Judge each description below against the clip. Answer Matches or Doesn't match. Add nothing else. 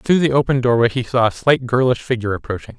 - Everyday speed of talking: Doesn't match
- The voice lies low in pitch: Matches